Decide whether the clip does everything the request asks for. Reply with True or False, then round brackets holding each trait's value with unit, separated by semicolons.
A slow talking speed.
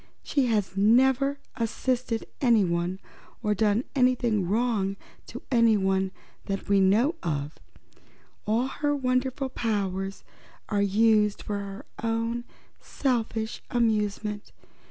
True (100 wpm)